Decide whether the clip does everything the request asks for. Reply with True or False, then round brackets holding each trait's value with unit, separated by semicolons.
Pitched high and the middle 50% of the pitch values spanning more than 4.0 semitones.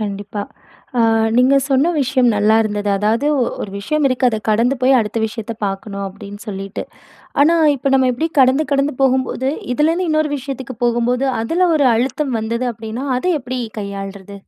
True (245 Hz; 4.4 semitones)